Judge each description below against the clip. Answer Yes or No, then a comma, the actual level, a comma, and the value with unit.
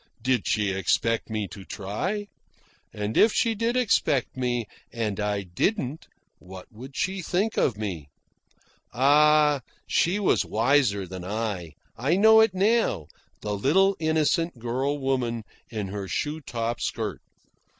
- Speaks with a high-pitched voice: No, low, 125 Hz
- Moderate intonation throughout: No, wide, 7.5 semitones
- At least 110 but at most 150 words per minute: Yes, average, 140 wpm